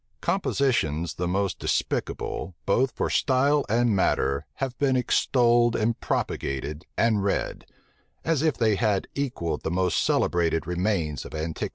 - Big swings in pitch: Yes, wide, 7.0 semitones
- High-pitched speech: No, low, 105 Hz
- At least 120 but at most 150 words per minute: Yes, average, 140 wpm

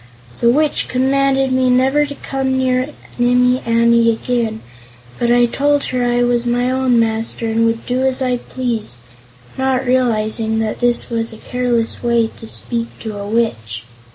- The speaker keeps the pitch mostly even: Yes, narrow, 2.1 semitones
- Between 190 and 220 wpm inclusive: No, average, 165 wpm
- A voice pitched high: Yes, high, 245 Hz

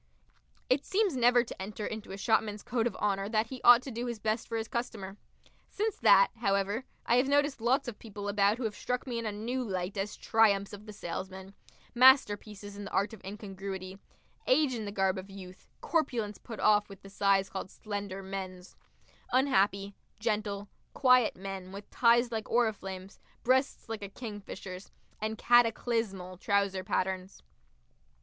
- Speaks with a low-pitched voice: No, high, 210 Hz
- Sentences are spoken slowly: No, average, 170 wpm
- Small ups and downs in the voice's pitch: No, average, 3.5 semitones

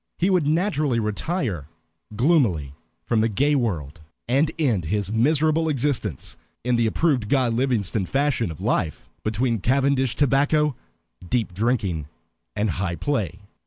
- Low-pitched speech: Yes, low, 120 Hz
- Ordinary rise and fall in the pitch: No, wide, 5.9 semitones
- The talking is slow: Yes, slow, 130 wpm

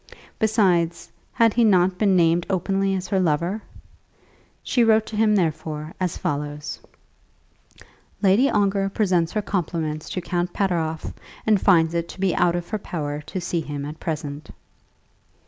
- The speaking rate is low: No, average, 150 wpm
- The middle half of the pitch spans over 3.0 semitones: Yes, average, 3.5 semitones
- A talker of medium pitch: Yes, medium, 180 Hz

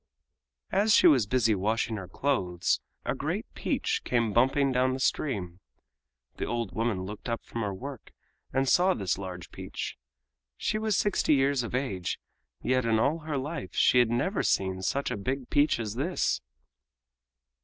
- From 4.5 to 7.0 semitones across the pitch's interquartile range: Yes, average, 5.1 semitones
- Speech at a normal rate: Yes, average, 165 wpm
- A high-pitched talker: No, low, 125 Hz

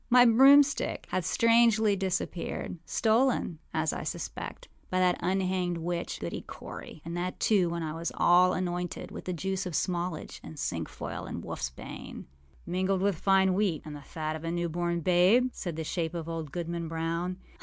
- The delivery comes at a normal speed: Yes, average, 175 wpm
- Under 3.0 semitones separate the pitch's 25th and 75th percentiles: Yes, narrow, 2.6 semitones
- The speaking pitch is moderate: Yes, medium, 175 Hz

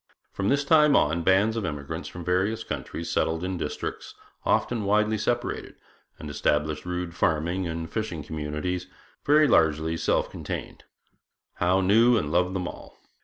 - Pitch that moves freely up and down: No, average, 4.8 semitones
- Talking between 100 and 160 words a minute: Yes, average, 150 wpm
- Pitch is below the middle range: Yes, very low, 90 Hz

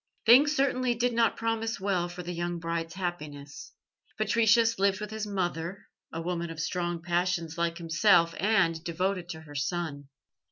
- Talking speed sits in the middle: Yes, average, 160 wpm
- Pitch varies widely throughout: No, average, 4.3 semitones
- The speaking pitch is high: No, medium, 175 Hz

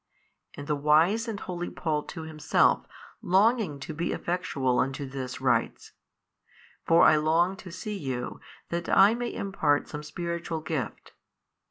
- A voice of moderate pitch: Yes, medium, 165 Hz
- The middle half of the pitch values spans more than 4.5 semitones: No, average, 3.9 semitones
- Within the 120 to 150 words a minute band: Yes, average, 145 wpm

